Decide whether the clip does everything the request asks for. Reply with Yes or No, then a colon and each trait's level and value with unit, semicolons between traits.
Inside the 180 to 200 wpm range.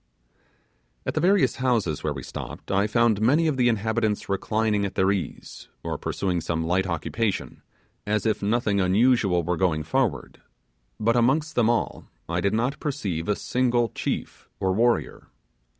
No: average, 160 wpm